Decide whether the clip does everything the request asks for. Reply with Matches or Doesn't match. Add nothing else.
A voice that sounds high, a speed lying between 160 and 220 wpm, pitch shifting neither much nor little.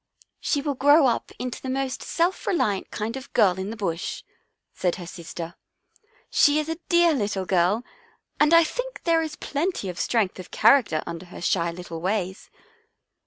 Doesn't match